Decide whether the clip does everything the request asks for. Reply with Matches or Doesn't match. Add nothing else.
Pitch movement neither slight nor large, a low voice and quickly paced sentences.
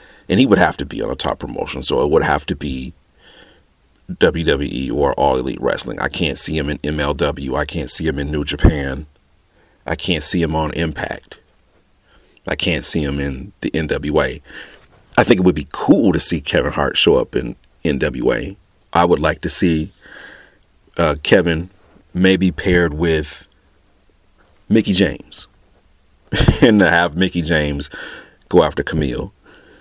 Doesn't match